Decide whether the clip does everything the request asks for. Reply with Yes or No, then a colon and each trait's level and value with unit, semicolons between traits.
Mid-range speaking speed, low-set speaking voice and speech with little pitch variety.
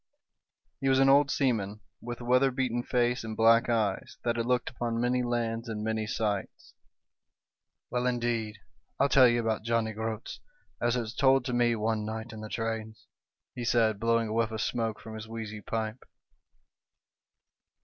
Yes: average, 170 wpm; low, 115 Hz; narrow, 1.7 semitones